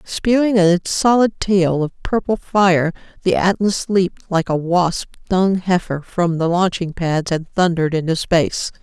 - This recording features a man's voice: No, female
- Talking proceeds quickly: No, average, 155 wpm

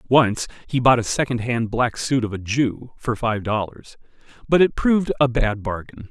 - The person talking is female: No, male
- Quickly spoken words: No, average, 185 wpm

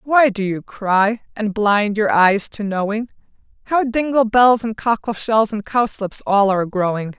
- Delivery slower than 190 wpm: Yes, average, 175 wpm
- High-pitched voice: Yes, high, 215 Hz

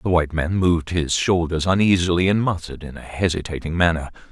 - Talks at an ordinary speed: Yes, average, 180 wpm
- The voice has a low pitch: Yes, very low, 85 Hz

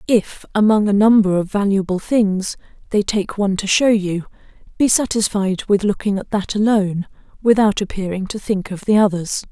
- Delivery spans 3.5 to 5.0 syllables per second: No, 5.2 syllables/s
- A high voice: Yes, high, 200 Hz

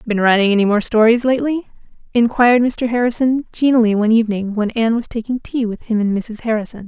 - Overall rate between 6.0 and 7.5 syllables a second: Yes, 6.4 syllables/s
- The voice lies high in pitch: Yes, high, 230 Hz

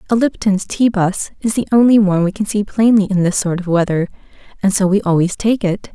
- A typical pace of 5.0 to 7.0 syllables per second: Yes, 5.8 syllables/s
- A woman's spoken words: Yes, female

